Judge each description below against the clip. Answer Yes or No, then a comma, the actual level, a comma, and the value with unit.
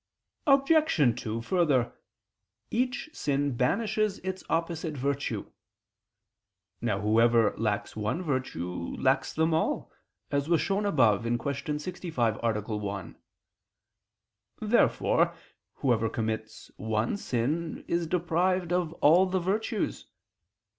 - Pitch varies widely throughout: Yes, wide, 7.7 semitones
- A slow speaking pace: Yes, slow, 105 wpm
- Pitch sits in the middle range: Yes, medium, 145 Hz